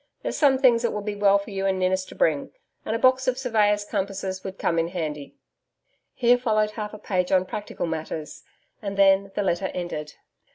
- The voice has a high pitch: Yes, high, 200 Hz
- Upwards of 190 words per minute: Yes, fast, 205 wpm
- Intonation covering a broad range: No, average, 2.8 semitones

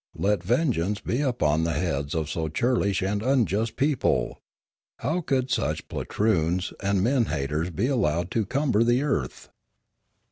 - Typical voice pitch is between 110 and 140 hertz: No, low, 100 Hz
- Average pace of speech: Yes, average, 150 wpm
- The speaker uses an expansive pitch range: Yes, wide, 7.2 semitones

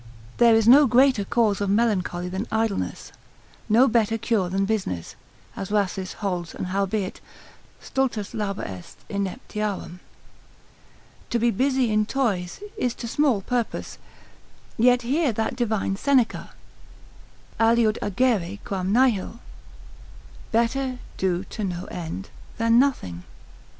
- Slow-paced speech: Yes, slow, 120 wpm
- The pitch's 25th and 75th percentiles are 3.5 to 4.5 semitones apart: Yes, average, 3.8 semitones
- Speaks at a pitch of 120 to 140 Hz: No, high, 215 Hz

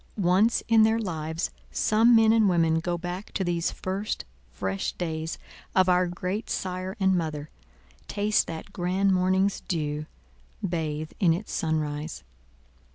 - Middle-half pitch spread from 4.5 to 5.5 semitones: No, average, 3.6 semitones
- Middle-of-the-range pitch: Yes, medium, 175 Hz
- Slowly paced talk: Yes, slow, 130 wpm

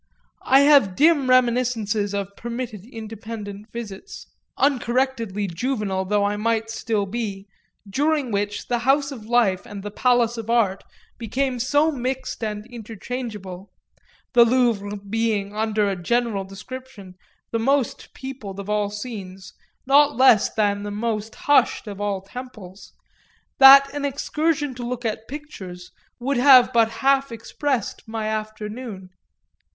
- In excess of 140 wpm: No, slow, 135 wpm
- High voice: Yes, high, 225 Hz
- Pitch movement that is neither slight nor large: Yes, average, 3.8 semitones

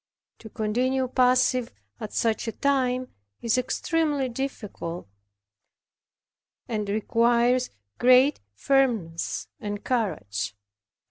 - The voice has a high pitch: Yes, high, 245 Hz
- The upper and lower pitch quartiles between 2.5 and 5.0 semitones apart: Yes, average, 3.3 semitones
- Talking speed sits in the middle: No, slow, 85 wpm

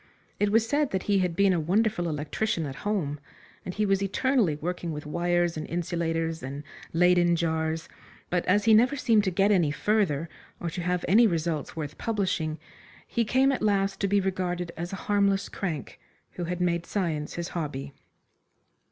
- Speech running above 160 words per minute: Yes, average, 180 wpm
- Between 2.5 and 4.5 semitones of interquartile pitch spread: Yes, average, 3.8 semitones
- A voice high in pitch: No, medium, 180 Hz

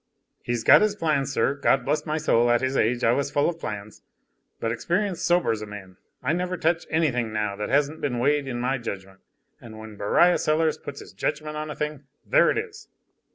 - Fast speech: Yes, fast, 215 wpm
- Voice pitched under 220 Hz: Yes, medium, 140 Hz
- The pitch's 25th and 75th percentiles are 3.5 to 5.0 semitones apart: No, wide, 5.6 semitones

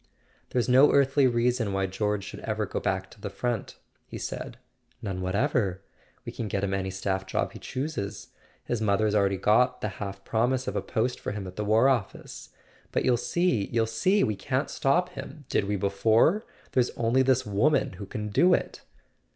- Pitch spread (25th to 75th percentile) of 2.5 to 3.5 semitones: No, average, 4.5 semitones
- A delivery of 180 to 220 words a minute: Yes, average, 190 wpm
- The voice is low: Yes, low, 110 Hz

